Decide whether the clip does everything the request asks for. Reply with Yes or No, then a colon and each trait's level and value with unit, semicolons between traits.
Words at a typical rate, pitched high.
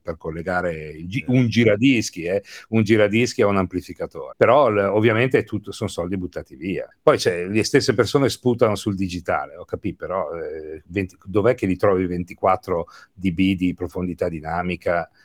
No: average, 140 wpm; low, 100 Hz